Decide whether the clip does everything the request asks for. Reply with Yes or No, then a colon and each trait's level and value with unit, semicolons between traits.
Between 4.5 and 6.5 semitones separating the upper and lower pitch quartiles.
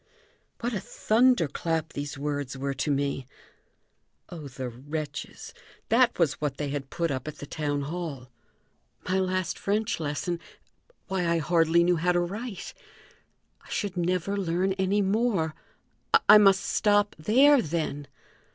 Yes: average, 5.1 semitones